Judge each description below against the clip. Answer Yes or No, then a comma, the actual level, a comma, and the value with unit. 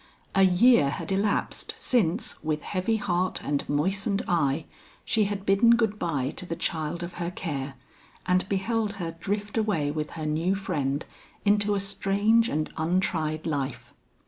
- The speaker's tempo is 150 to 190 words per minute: Yes, average, 155 wpm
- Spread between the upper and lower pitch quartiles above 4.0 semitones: Yes, average, 4.6 semitones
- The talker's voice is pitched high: No, medium, 180 Hz